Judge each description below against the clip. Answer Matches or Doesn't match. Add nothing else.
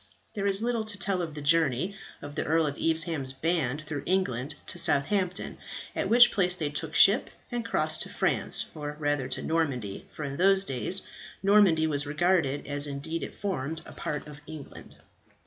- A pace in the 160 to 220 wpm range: Matches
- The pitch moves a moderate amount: Matches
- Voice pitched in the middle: Matches